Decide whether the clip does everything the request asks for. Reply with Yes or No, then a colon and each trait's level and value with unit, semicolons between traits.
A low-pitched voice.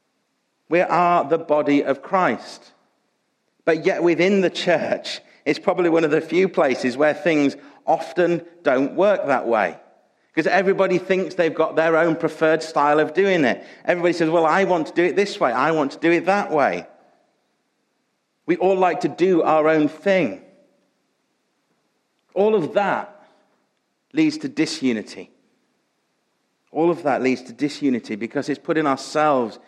No: medium, 165 Hz